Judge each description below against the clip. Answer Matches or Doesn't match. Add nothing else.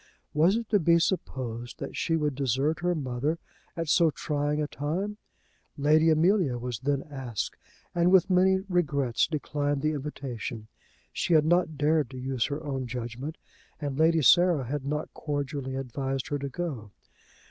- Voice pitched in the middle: Matches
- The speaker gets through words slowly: Doesn't match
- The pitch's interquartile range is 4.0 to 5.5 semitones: Doesn't match